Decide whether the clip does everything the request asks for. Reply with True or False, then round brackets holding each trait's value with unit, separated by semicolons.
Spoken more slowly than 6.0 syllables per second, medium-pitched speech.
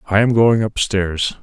False (4.2 syllables/s; 105 Hz)